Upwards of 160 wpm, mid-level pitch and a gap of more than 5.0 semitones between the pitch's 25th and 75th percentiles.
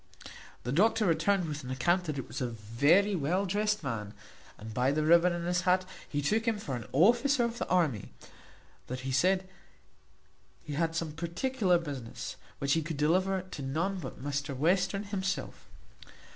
Yes: average, 175 wpm; medium, 165 Hz; wide, 5.4 semitones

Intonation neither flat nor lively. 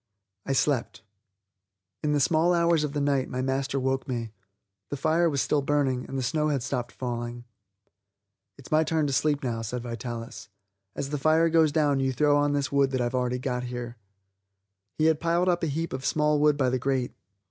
Yes: average, 3.3 semitones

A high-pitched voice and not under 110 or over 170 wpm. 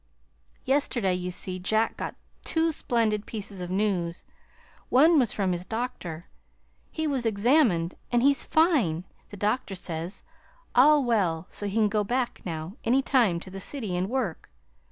Yes: high, 210 Hz; average, 155 wpm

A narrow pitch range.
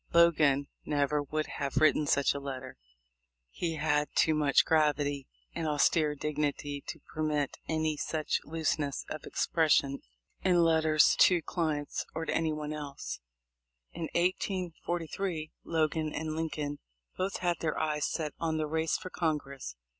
Yes: narrow, 1.8 semitones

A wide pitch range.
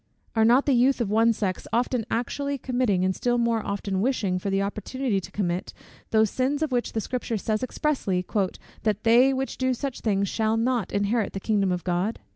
No: average, 4.0 semitones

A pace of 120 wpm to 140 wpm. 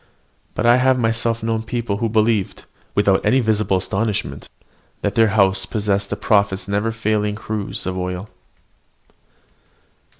Yes: slow, 135 wpm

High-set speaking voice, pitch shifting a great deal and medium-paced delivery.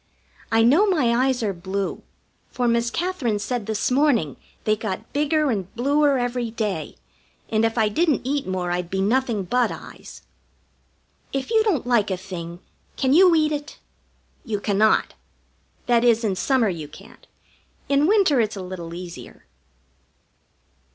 Yes: high, 235 Hz; wide, 5.8 semitones; average, 155 wpm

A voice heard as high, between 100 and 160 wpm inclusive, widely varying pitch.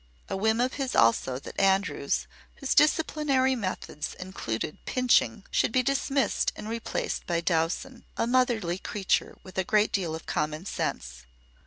Yes: high, 205 Hz; average, 150 wpm; wide, 7.1 semitones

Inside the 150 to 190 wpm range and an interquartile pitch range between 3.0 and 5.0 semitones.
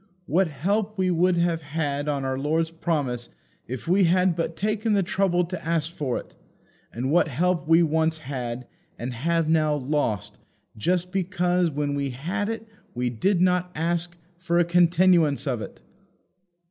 Yes: average, 165 wpm; average, 3.8 semitones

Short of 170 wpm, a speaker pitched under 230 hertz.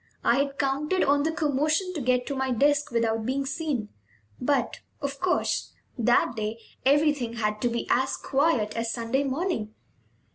No: average, 160 wpm; very high, 270 Hz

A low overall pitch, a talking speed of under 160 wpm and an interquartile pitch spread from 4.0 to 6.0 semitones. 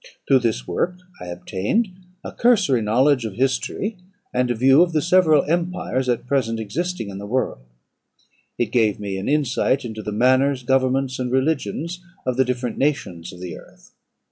No: low, 130 Hz; average, 170 wpm; average, 4.9 semitones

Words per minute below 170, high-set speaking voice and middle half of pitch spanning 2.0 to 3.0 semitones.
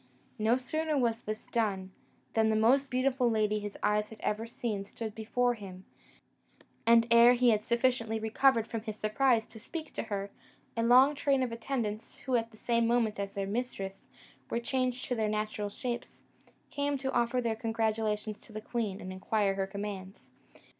No: average, 180 wpm; high, 225 Hz; narrow, 2.6 semitones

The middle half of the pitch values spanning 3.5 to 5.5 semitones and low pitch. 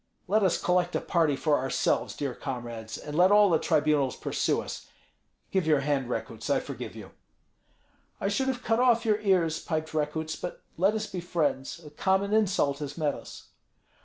No: average, 5.2 semitones; medium, 165 Hz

